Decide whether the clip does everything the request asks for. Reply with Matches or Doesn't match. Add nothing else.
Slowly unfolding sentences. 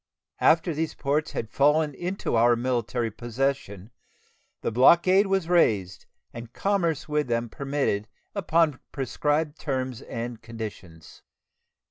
Matches